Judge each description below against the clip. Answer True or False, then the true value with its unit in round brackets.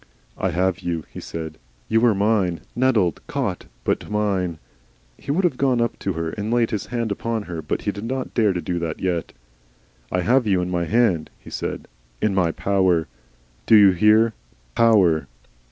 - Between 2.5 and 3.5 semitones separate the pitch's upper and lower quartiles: False (4.5 semitones)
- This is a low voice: True (100 Hz)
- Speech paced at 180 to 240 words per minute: True (185 wpm)